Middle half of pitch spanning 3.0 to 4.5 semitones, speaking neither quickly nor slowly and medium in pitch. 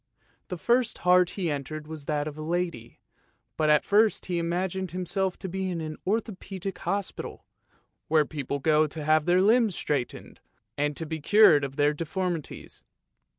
Yes: average, 3.8 semitones; average, 170 wpm; medium, 170 Hz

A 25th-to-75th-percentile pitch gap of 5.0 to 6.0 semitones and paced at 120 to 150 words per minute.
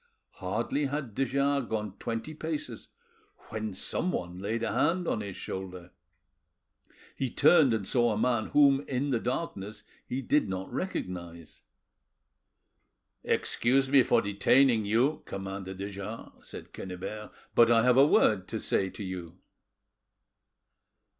Yes: wide, 5.6 semitones; slow, 135 wpm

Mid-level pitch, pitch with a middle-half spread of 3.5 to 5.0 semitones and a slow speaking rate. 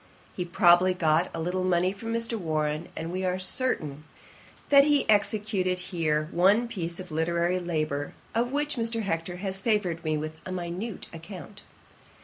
No: medium, 180 Hz; average, 3.9 semitones; average, 160 wpm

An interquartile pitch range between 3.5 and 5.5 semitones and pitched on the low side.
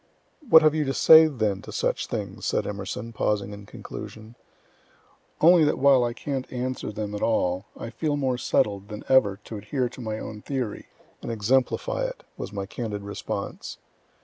Yes: average, 4.8 semitones; low, 115 Hz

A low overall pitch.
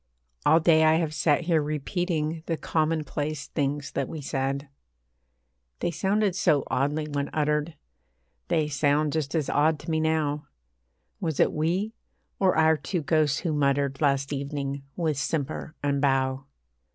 No: medium, 150 Hz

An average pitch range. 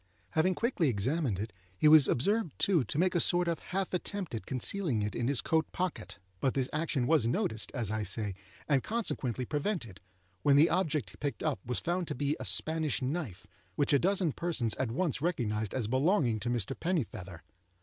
No: wide, 6.6 semitones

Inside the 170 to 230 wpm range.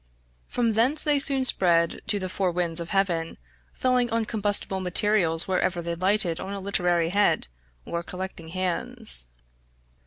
No: average, 150 wpm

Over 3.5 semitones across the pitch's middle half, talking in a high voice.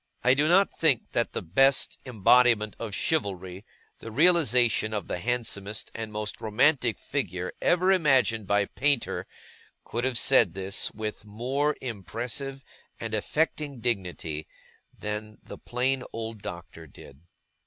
No: average, 4.6 semitones; low, 115 Hz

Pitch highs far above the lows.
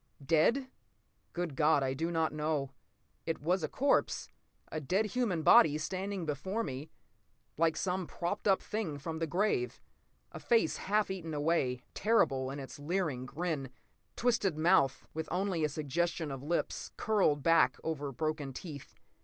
No: average, 4.4 semitones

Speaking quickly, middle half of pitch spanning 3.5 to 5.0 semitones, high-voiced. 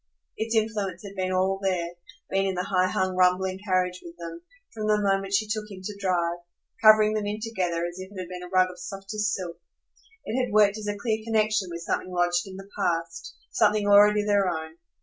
No: fast, 215 wpm; narrow, 2.6 semitones; high, 195 Hz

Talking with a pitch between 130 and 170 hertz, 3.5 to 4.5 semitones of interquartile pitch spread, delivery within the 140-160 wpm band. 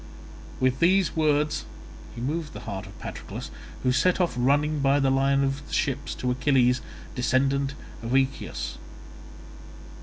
No: low, 135 Hz; narrow, 2.5 semitones; average, 145 wpm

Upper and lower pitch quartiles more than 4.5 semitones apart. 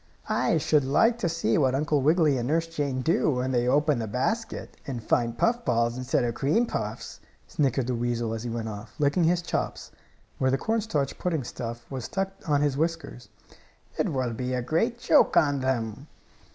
Yes: average, 4.9 semitones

